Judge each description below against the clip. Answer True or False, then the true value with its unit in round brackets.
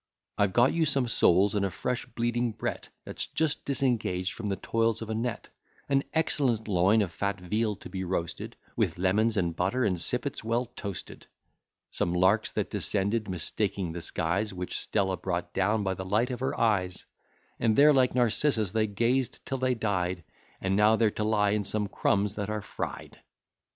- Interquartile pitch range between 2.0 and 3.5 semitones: False (3.9 semitones)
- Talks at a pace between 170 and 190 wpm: True (185 wpm)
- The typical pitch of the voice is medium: False (105 Hz)